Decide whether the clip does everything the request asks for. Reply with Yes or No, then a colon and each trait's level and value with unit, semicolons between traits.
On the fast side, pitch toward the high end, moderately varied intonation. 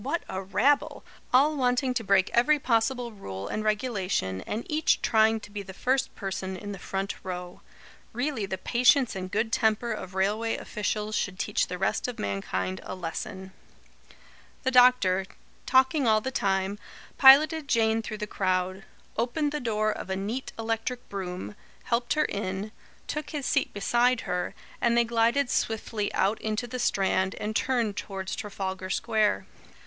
No: average, 165 wpm; high, 215 Hz; average, 4.4 semitones